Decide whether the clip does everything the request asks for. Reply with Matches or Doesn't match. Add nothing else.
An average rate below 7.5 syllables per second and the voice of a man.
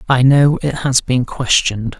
Matches